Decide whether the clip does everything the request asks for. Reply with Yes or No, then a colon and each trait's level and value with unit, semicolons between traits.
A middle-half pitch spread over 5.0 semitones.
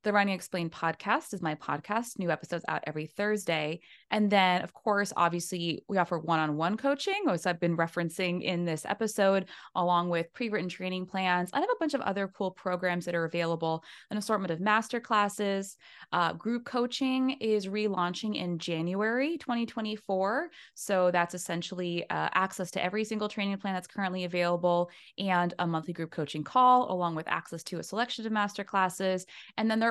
No: average, 3.5 semitones